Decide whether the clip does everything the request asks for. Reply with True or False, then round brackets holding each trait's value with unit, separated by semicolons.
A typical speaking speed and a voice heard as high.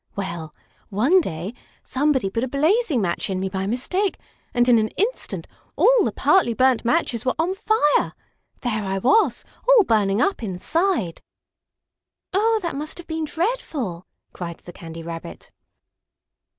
True (150 wpm; 250 Hz)